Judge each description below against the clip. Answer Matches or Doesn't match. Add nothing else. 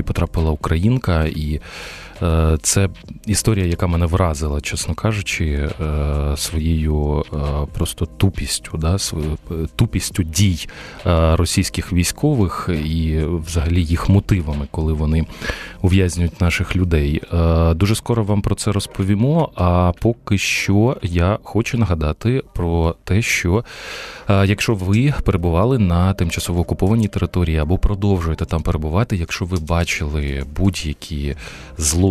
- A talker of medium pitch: Doesn't match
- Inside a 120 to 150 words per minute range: Doesn't match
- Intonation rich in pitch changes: Doesn't match